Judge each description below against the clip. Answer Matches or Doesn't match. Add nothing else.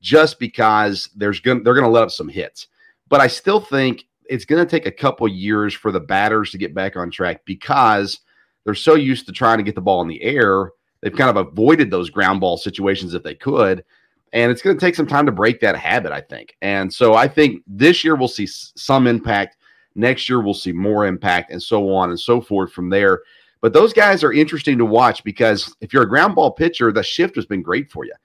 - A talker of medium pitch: Doesn't match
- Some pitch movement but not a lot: Doesn't match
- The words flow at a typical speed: Doesn't match